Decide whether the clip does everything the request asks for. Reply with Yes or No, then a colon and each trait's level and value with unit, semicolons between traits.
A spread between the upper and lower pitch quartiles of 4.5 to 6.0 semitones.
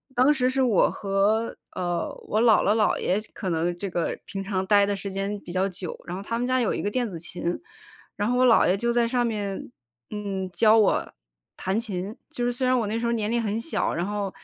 No: average, 3.5 semitones